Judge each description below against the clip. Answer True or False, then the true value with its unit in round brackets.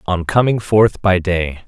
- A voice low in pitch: True (95 Hz)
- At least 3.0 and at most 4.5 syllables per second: True (4.0 syllables/s)